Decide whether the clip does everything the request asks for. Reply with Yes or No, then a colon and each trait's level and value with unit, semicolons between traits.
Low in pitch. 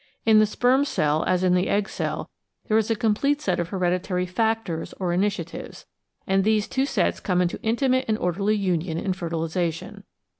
No: high, 195 Hz